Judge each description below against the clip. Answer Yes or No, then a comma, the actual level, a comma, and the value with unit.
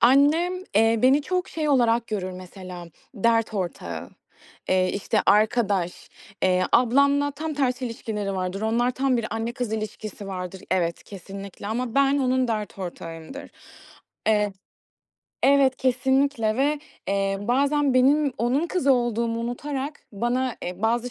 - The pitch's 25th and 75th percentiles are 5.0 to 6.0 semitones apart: Yes, average, 5.3 semitones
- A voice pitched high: Yes, high, 235 Hz